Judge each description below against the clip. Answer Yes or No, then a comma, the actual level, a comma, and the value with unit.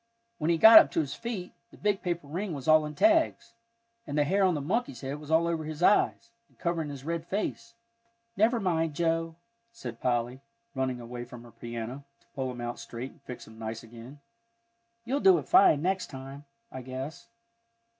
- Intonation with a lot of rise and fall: Yes, wide, 5.7 semitones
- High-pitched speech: No, medium, 150 Hz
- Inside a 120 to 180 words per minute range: No, average, 200 wpm